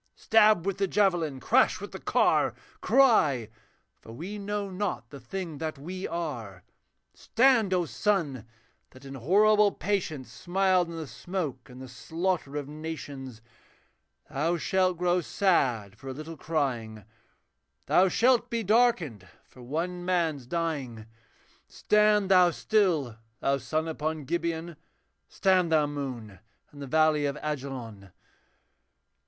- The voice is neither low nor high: Yes, medium, 160 Hz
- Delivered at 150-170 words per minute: No, slow, 135 wpm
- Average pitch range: No, wide, 5.9 semitones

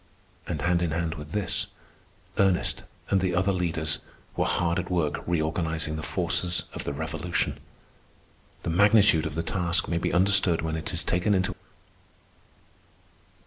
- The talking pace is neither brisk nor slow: Yes, average, 150 wpm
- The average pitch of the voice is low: Yes, very low, 85 Hz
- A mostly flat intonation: Yes, narrow, 2.3 semitones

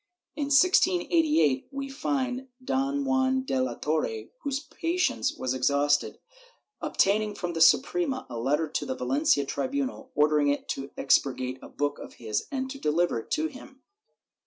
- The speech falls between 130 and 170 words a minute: Yes, average, 150 wpm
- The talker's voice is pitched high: Yes, very high, 255 Hz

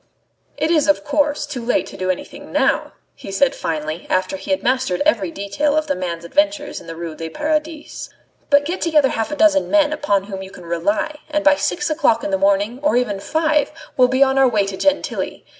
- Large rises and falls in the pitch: Yes, wide, 7.5 semitones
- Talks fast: Yes, fast, 220 wpm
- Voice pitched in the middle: No, very high, 260 Hz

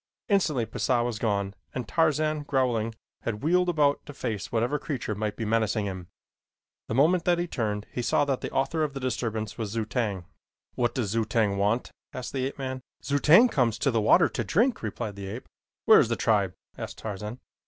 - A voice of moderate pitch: No, low, 120 Hz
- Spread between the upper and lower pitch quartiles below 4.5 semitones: No, average, 4.8 semitones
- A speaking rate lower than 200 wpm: No, fast, 205 wpm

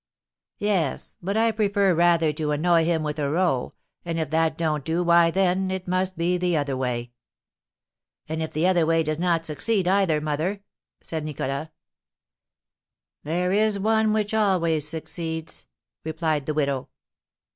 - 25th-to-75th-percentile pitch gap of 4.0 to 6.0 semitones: No, average, 3.3 semitones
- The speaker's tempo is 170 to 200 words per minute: No, average, 155 wpm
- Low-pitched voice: No, medium, 165 Hz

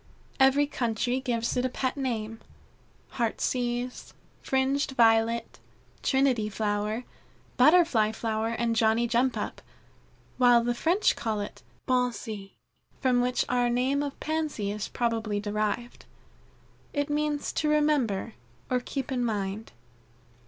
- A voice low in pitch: No, high, 240 Hz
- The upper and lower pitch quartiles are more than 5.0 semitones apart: No, average, 3.1 semitones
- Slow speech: Yes, slow, 120 wpm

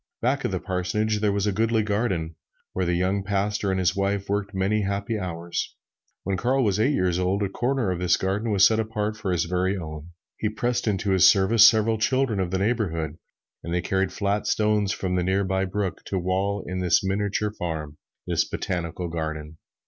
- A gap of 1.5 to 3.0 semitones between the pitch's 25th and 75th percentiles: Yes, narrow, 2.6 semitones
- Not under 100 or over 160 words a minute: No, fast, 205 wpm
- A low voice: Yes, very low, 95 Hz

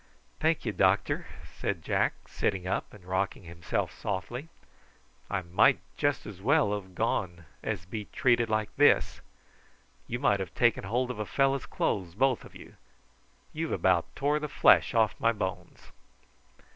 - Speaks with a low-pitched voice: Yes, low, 105 Hz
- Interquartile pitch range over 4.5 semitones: Yes, average, 5.1 semitones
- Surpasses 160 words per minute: No, average, 155 wpm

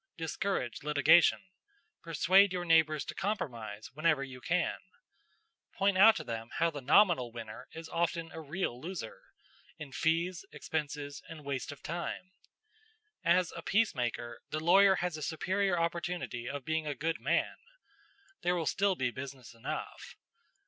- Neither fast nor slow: Yes, average, 145 wpm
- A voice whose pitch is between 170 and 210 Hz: No, medium, 160 Hz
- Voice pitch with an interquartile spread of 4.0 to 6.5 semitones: Yes, average, 4.4 semitones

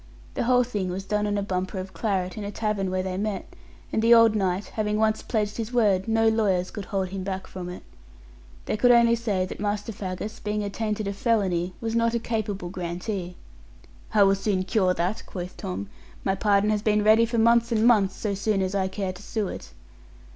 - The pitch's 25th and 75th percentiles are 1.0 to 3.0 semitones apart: Yes, average, 2.7 semitones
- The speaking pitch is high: Yes, high, 205 Hz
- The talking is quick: Yes, fast, 215 wpm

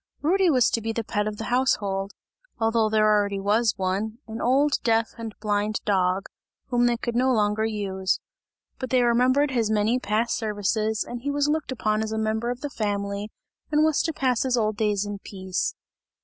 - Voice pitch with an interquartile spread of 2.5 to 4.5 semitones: Yes, average, 3.0 semitones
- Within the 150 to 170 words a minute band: No, average, 195 wpm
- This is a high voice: Yes, high, 220 Hz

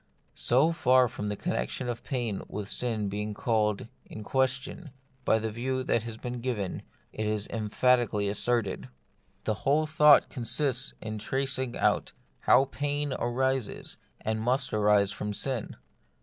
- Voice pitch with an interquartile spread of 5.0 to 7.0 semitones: No, average, 3.7 semitones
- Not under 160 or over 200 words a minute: No, average, 145 wpm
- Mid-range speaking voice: No, low, 120 Hz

